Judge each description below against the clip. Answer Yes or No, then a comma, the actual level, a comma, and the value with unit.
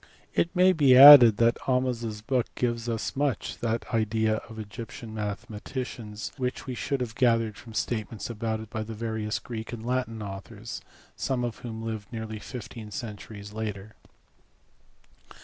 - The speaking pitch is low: Yes, low, 115 Hz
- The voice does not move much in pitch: Yes, narrow, 2.2 semitones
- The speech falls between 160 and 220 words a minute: No, average, 150 wpm